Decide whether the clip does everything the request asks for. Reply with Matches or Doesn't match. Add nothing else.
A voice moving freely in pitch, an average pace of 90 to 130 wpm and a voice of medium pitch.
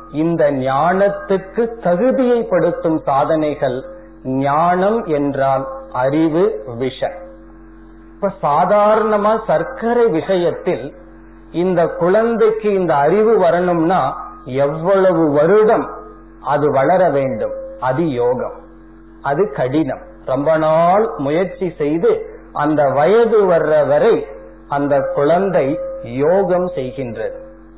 Doesn't match